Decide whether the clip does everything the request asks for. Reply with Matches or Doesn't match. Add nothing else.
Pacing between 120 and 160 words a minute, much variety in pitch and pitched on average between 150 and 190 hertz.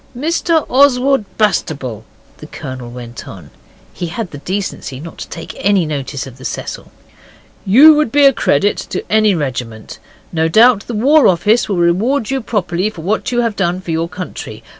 Doesn't match